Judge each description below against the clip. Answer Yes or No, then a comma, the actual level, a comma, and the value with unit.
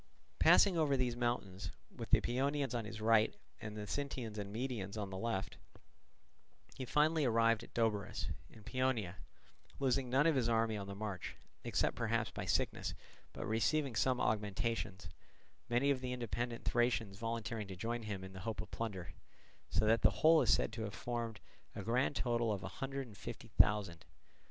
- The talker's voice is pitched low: Yes, low, 115 Hz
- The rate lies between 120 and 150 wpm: No, average, 180 wpm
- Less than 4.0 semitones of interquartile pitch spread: Yes, average, 3.2 semitones